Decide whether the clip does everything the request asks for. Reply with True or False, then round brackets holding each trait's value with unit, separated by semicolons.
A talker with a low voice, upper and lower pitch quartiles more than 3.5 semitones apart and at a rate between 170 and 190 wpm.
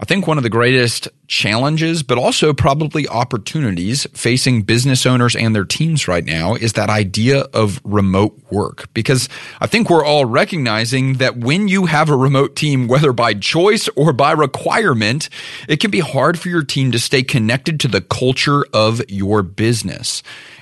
True (130 Hz; 5.1 semitones; 175 wpm)